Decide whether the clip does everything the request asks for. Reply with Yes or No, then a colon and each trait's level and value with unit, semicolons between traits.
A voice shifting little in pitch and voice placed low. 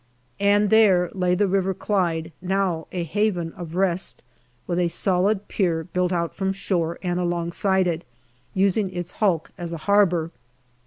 No: narrow, 2.2 semitones; medium, 180 Hz